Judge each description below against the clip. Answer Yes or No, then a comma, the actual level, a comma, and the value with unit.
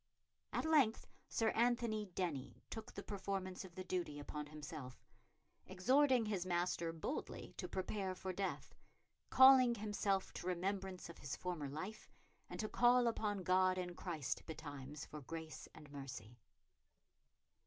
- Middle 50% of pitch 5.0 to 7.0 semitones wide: Yes, wide, 5.4 semitones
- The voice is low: No, medium, 185 Hz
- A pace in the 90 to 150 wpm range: Yes, average, 140 wpm